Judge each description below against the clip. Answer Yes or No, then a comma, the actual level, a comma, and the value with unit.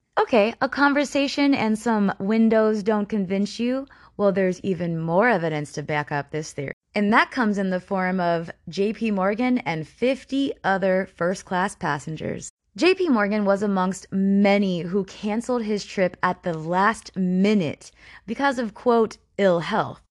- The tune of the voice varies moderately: Yes, average, 3.7 semitones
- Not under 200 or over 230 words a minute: No, average, 160 wpm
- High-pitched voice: Yes, high, 200 Hz